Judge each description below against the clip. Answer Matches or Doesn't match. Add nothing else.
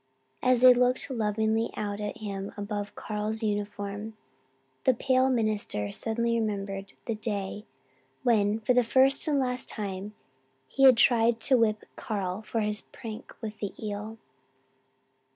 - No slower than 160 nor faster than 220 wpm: Doesn't match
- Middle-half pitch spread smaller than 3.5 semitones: Matches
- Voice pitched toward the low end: Doesn't match